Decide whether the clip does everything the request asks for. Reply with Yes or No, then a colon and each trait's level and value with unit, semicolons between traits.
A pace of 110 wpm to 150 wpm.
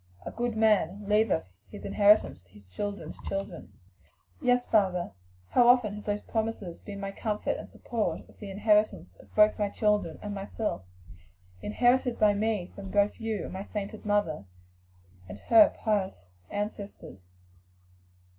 Yes: average, 145 wpm